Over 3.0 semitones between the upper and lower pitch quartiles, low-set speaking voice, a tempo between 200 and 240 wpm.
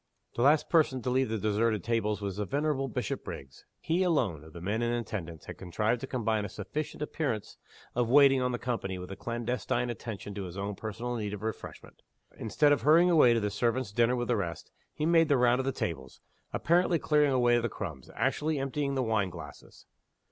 Yes: average, 4.8 semitones; low, 120 Hz; fast, 205 wpm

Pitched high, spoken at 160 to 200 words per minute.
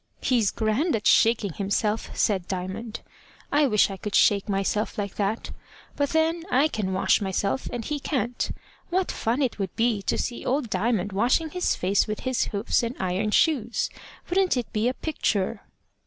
Yes: high, 225 Hz; average, 175 wpm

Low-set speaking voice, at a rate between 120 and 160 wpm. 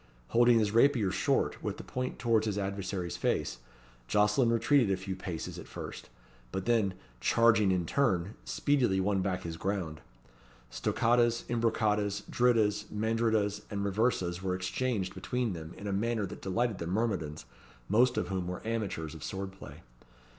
Yes: low, 105 Hz; average, 155 wpm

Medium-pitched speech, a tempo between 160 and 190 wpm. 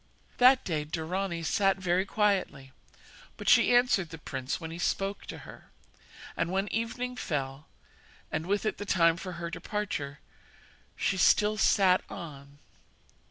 No: medium, 180 Hz; average, 145 wpm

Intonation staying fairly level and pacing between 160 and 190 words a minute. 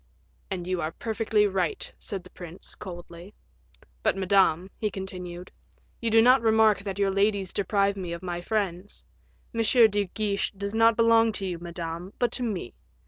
No: average, 3.5 semitones; average, 170 wpm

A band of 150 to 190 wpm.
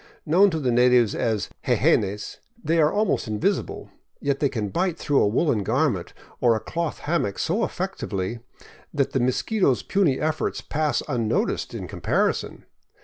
Yes: average, 155 wpm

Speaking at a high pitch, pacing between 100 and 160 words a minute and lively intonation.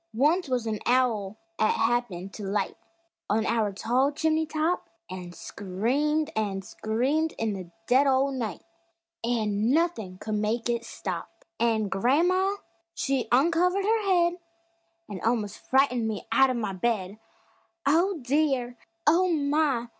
Yes: high, 245 Hz; average, 140 wpm; wide, 6.1 semitones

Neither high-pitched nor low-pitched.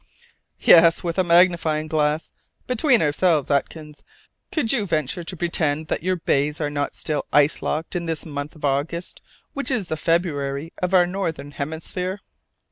Yes: medium, 160 Hz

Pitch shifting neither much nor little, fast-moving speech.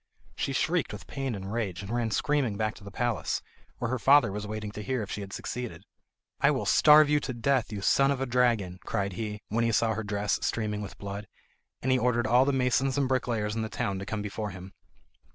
Yes: average, 3.7 semitones; fast, 235 wpm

